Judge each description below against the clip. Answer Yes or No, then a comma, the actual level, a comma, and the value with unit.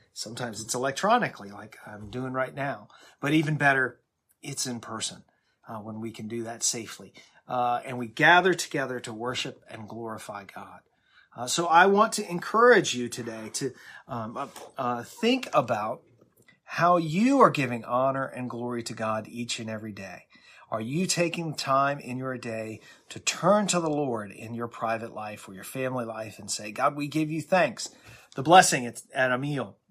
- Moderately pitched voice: No, low, 125 Hz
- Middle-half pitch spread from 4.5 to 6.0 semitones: Yes, average, 5.2 semitones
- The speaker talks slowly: No, average, 185 wpm